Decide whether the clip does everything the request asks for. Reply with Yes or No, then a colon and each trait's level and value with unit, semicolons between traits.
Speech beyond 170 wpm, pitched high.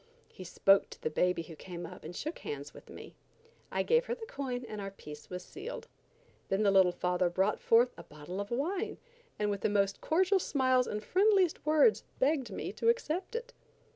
Yes: average, 200 wpm; high, 215 Hz